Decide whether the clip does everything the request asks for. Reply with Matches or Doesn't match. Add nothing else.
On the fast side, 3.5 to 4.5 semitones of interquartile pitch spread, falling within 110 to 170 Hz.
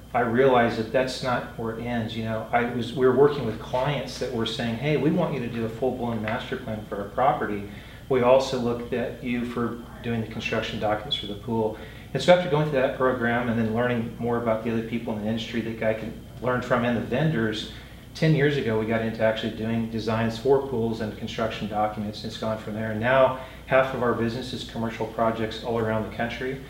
Doesn't match